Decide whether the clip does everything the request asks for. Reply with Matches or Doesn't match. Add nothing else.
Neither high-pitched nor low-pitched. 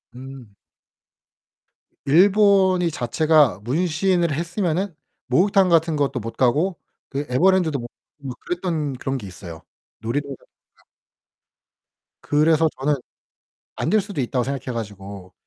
Matches